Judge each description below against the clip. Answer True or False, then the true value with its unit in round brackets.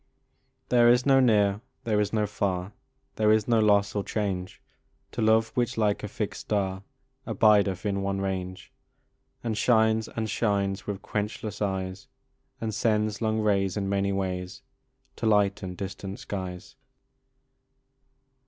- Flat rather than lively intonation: True (2.0 semitones)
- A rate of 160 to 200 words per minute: False (140 wpm)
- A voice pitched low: True (105 Hz)